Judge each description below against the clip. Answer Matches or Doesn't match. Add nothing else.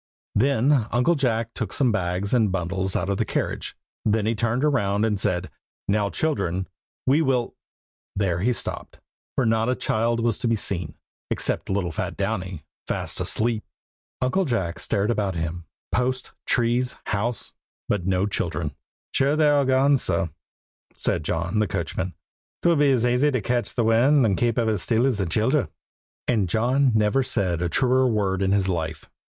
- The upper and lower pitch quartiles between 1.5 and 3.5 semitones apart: Doesn't match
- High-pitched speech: Doesn't match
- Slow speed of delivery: Doesn't match